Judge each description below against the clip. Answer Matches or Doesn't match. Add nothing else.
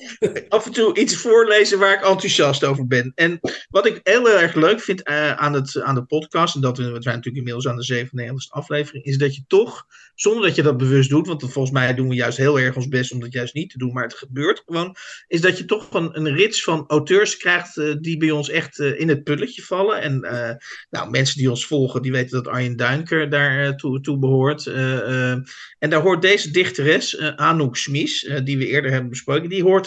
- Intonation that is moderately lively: Matches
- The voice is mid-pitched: Matches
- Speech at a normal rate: Doesn't match